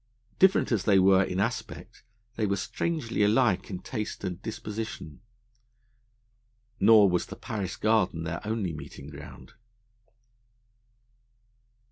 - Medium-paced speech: No, slow, 115 wpm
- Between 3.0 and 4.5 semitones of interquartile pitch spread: Yes, average, 3.4 semitones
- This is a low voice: Yes, low, 100 Hz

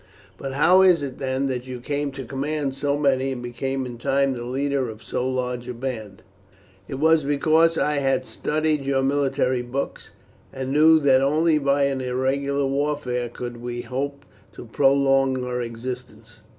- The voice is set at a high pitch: No, low, 135 Hz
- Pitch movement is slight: Yes, narrow, 2.1 semitones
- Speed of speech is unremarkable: Yes, average, 170 wpm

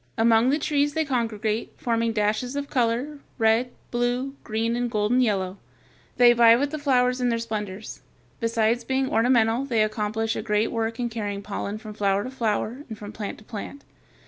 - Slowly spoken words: No, average, 180 wpm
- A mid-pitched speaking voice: No, high, 230 Hz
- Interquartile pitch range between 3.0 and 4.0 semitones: No, narrow, 2.5 semitones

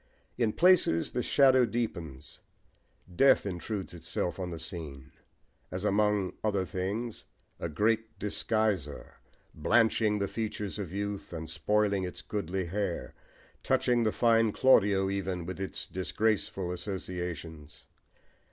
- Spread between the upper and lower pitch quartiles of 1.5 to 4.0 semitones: Yes, average, 3.6 semitones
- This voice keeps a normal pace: No, slow, 120 wpm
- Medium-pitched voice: No, low, 100 Hz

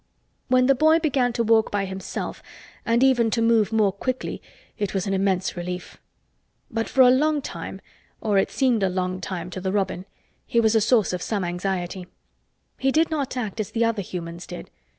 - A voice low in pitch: No, high, 215 Hz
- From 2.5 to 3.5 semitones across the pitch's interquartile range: No, average, 4.8 semitones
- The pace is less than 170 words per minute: No, average, 190 wpm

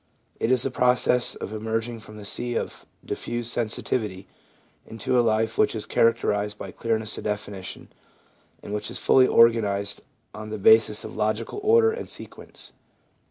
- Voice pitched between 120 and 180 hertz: No, low, 110 Hz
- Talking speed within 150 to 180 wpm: Yes, average, 160 wpm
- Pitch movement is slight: Yes, narrow, 2.3 semitones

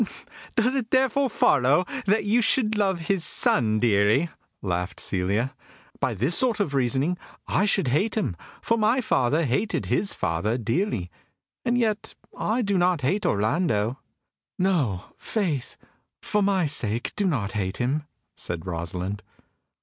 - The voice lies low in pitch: No, medium, 155 Hz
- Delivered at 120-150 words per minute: Yes, average, 140 wpm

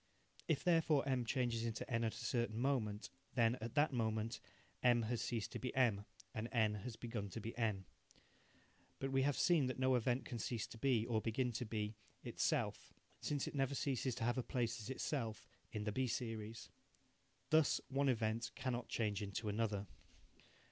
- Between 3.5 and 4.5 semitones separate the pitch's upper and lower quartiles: No, average, 2.9 semitones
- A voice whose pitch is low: Yes, low, 115 Hz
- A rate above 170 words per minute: Yes, average, 185 wpm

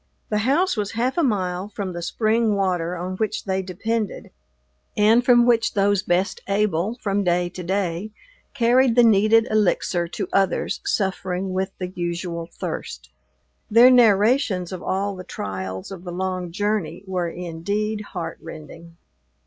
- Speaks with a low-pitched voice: No, high, 195 Hz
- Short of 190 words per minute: Yes, average, 150 wpm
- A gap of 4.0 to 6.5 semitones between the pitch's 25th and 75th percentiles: No, average, 3.5 semitones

